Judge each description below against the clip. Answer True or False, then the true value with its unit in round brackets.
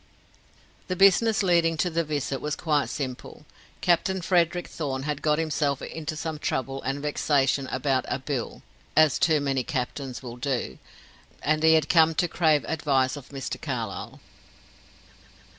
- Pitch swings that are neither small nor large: True (3.2 semitones)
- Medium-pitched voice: True (150 Hz)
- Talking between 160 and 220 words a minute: False (150 wpm)